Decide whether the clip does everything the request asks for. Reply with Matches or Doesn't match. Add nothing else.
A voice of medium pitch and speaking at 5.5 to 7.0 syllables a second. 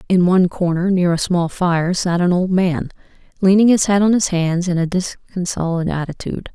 Doesn't match